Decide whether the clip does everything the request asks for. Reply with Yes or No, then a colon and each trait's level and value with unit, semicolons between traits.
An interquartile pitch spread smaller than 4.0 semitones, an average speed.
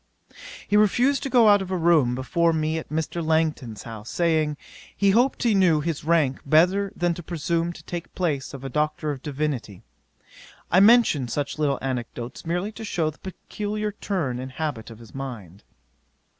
No: wide, 5.4 semitones; average, 180 wpm